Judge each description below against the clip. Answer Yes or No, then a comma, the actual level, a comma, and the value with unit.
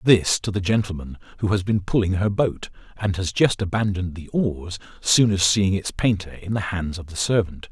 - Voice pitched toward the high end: No, very low, 95 Hz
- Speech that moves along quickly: Yes, fast, 210 wpm